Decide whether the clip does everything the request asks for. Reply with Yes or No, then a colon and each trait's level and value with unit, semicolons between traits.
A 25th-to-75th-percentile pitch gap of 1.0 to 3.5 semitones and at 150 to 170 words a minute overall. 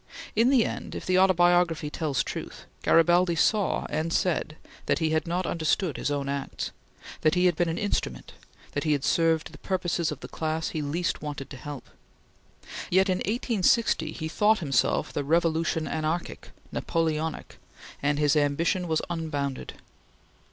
Yes: average, 2.8 semitones; average, 160 wpm